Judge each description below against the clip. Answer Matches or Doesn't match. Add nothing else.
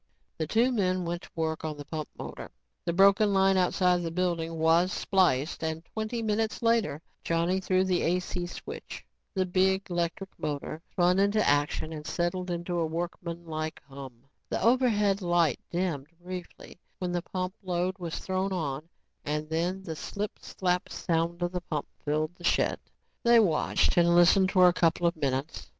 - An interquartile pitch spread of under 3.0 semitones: Matches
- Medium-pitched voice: Matches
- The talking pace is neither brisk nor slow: Matches